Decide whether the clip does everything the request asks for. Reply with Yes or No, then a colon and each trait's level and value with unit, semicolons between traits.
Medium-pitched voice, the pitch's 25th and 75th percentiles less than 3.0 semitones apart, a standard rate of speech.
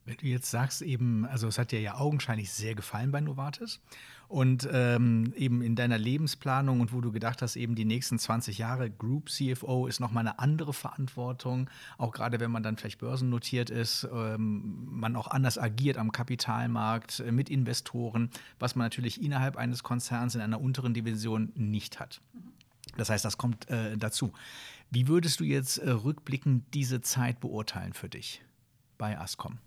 No: low, 120 Hz; narrow, 2.4 semitones; average, 175 wpm